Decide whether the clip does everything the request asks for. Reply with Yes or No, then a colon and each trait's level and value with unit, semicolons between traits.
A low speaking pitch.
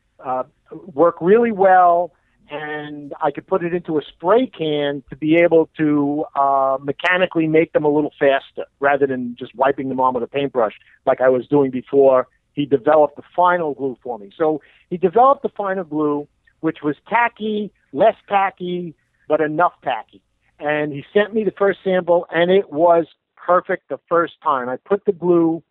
No: medium, 155 Hz